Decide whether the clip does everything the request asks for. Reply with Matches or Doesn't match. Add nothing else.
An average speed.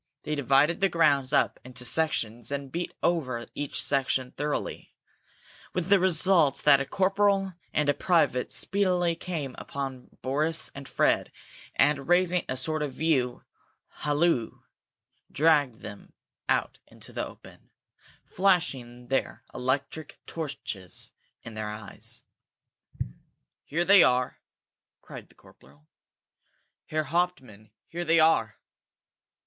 Doesn't match